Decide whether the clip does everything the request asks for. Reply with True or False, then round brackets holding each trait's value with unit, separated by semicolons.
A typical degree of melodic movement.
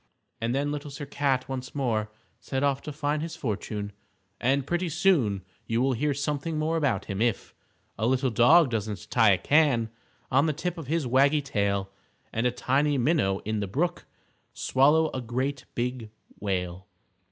True (4.6 semitones)